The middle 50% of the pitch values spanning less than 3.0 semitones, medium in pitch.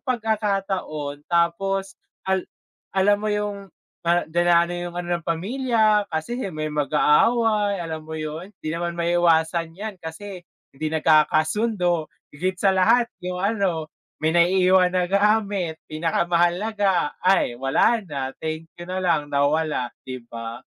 No: average, 4.0 semitones; medium, 175 Hz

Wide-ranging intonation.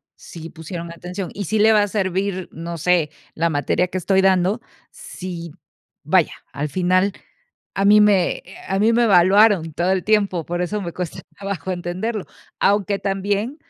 No: average, 2.8 semitones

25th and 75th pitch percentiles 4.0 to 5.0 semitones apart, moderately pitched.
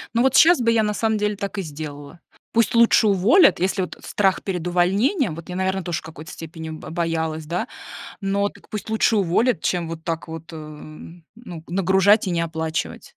Yes: average, 4.4 semitones; medium, 180 Hz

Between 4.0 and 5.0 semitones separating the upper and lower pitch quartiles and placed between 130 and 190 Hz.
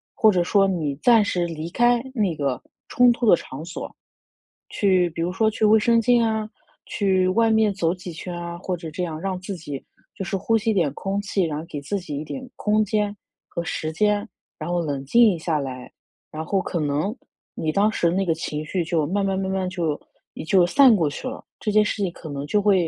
Yes: average, 4.4 semitones; medium, 185 Hz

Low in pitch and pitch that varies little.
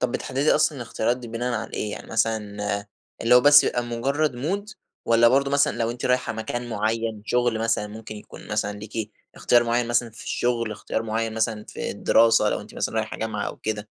Yes: low, 115 Hz; narrow, 1.9 semitones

